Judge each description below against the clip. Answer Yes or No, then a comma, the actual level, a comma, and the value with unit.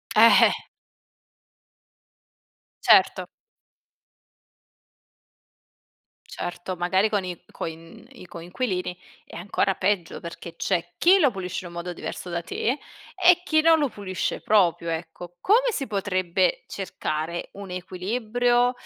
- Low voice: No, medium, 185 Hz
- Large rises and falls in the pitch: Yes, wide, 5.7 semitones